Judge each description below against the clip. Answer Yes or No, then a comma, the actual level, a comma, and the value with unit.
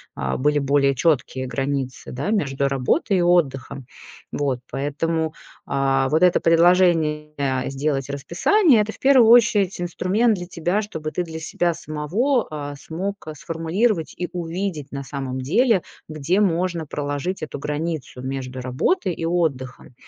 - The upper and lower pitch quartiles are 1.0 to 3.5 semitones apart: No, average, 4.7 semitones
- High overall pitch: No, medium, 160 Hz